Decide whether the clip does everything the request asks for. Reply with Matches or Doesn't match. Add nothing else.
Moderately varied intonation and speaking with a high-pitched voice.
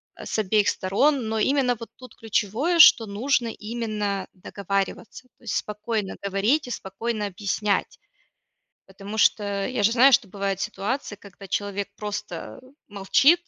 Matches